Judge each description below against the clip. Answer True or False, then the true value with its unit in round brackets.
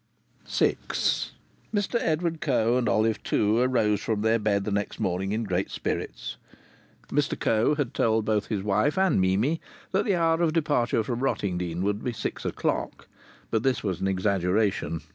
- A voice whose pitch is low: True (110 Hz)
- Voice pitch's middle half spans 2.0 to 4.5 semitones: False (5.2 semitones)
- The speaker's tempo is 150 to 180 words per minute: True (165 wpm)